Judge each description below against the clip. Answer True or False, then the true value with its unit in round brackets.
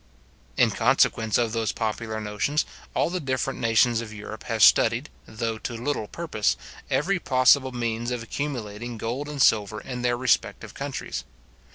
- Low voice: True (115 Hz)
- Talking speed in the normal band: True (155 wpm)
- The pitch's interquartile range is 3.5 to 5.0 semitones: False (3.0 semitones)